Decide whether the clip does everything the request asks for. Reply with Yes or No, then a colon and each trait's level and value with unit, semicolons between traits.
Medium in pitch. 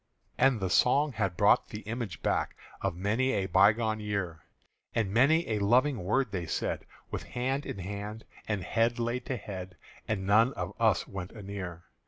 No: low, 105 Hz